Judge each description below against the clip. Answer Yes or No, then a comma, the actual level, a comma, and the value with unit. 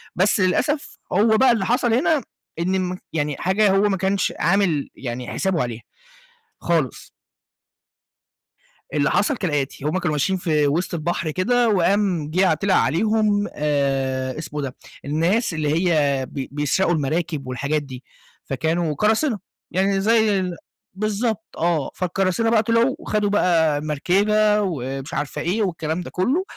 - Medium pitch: Yes, medium, 180 Hz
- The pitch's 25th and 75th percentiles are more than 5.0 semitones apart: Yes, wide, 5.5 semitones